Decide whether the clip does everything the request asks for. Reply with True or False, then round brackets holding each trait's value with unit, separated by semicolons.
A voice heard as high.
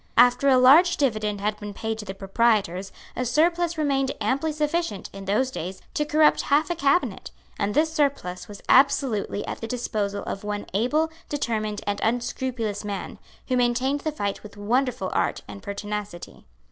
True (235 Hz)